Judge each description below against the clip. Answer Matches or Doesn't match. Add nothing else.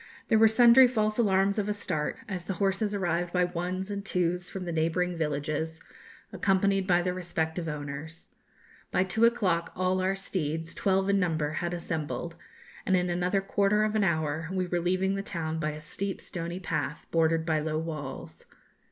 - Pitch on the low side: Doesn't match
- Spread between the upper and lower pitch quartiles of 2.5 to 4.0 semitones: Matches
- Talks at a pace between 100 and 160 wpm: Doesn't match